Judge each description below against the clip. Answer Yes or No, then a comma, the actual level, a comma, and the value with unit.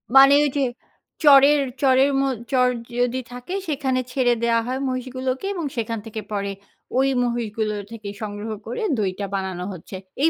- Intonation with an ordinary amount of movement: Yes, average, 3.8 semitones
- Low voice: No, high, 245 Hz